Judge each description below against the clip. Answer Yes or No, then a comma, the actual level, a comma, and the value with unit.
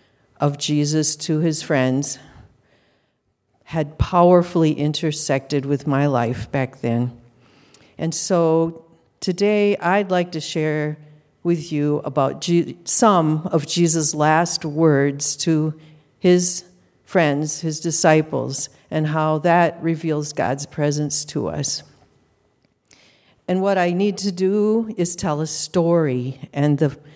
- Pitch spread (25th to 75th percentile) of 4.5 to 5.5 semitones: No, average, 3.0 semitones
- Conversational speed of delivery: No, slow, 115 wpm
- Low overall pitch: No, medium, 155 Hz